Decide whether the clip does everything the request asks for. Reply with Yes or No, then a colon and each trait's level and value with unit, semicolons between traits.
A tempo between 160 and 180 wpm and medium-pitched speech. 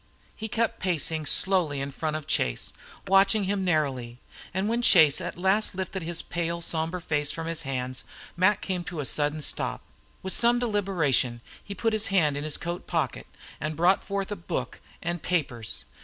Yes: average, 170 wpm; medium, 170 Hz